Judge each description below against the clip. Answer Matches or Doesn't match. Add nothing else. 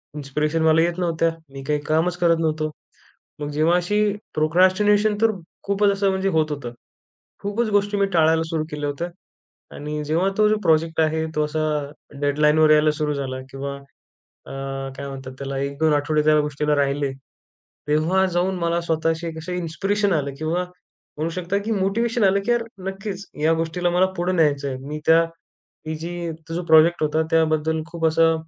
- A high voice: Doesn't match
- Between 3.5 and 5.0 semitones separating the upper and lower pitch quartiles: Doesn't match